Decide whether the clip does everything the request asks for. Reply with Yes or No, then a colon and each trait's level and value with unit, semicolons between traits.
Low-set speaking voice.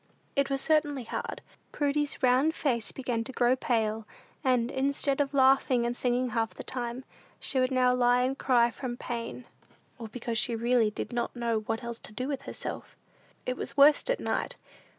No: very high, 250 Hz